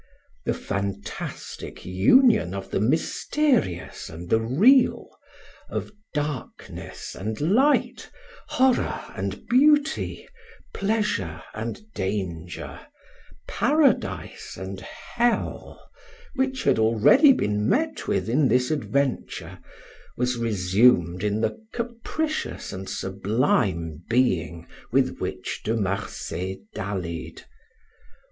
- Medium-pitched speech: No, low, 115 Hz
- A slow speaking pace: Yes, slow, 95 wpm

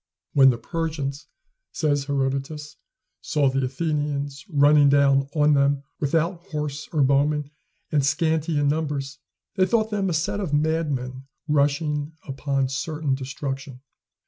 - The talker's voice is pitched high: No, medium, 145 Hz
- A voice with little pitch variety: Yes, narrow, 2.1 semitones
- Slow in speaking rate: Yes, slow, 130 wpm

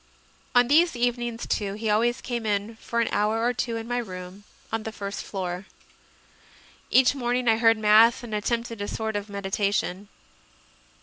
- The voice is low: No, high, 225 Hz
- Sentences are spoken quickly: No, average, 175 wpm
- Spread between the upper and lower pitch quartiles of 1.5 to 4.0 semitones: Yes, average, 2.7 semitones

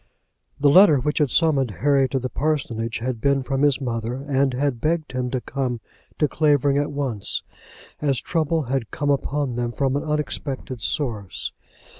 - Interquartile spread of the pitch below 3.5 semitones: Yes, average, 2.8 semitones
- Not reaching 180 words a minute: Yes, average, 170 wpm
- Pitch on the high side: No, low, 135 Hz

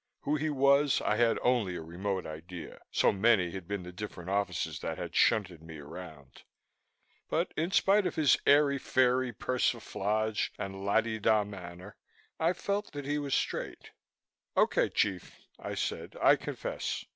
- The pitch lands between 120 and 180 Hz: No, low, 105 Hz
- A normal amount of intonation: No, wide, 7.1 semitones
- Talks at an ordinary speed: Yes, average, 160 wpm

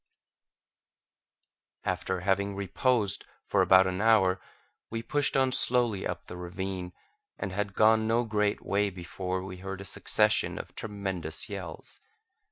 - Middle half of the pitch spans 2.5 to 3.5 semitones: Yes, average, 2.8 semitones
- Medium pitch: No, low, 100 Hz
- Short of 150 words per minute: Yes, slow, 135 wpm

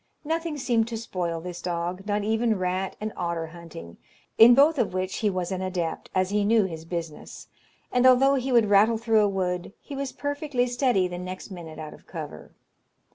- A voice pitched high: Yes, high, 200 Hz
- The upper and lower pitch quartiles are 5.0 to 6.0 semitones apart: Yes, average, 5.3 semitones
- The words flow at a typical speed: Yes, average, 195 wpm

